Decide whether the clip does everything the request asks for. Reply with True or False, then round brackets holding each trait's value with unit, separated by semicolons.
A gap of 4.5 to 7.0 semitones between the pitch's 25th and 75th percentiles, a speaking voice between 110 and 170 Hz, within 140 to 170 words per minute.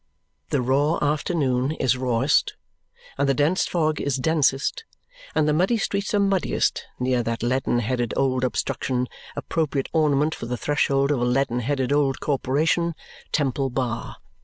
False (3.3 semitones; 140 Hz; 150 wpm)